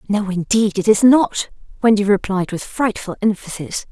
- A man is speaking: No, female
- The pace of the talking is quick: No, average, 155 wpm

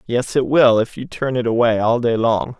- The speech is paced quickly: Yes, fast, 255 wpm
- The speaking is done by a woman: No, male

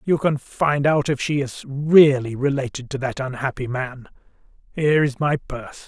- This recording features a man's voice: Yes, male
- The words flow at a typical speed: Yes, average, 175 wpm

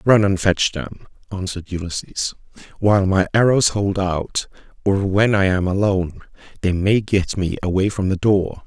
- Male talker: Yes, male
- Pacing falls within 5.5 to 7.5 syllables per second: No, 4.7 syllables/s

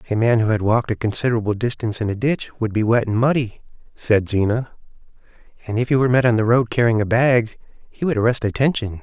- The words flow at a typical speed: No, fast, 220 wpm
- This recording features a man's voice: Yes, male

